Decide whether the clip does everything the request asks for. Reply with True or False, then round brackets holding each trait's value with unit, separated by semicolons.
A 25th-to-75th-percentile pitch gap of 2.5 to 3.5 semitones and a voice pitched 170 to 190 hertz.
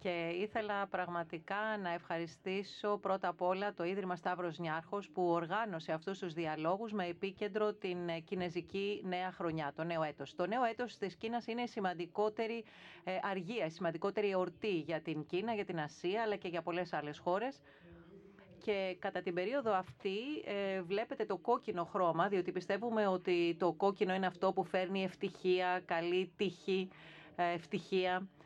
True (2.8 semitones; 185 Hz)